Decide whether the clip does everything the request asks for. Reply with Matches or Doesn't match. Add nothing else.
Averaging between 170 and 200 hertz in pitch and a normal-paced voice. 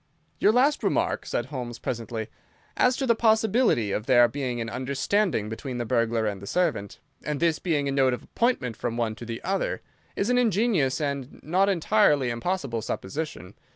Doesn't match